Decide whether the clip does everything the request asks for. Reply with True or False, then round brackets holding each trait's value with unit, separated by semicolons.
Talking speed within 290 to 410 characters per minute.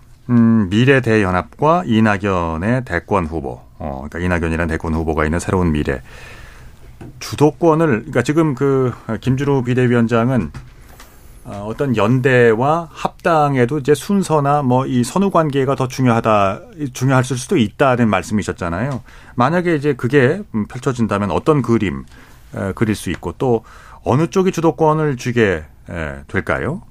True (295 characters per minute)